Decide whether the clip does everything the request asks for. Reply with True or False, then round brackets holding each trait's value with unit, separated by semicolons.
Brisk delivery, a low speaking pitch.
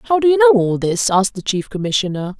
False (250 wpm; 205 Hz)